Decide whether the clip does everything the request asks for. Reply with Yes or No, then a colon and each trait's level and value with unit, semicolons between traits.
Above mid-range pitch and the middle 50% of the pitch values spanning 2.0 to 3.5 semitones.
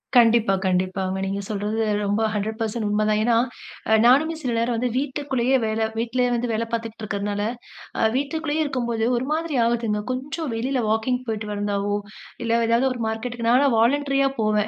Yes: high, 230 Hz; average, 3.2 semitones